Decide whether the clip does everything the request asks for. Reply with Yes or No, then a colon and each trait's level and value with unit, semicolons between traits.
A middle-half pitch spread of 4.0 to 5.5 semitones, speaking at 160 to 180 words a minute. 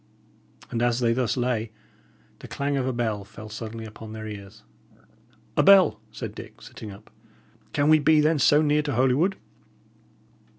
Yes: average, 5.0 semitones; average, 165 wpm